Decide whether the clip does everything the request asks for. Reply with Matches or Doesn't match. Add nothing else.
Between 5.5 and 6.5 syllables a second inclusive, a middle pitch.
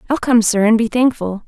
Doesn't match